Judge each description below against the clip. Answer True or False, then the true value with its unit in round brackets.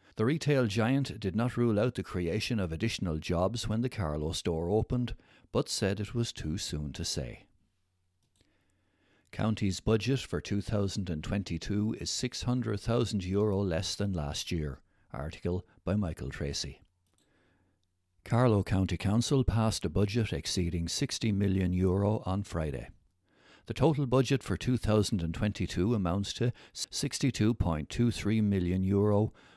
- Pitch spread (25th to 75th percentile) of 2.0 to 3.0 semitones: False (3.7 semitones)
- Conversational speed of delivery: False (120 wpm)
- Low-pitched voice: True (100 Hz)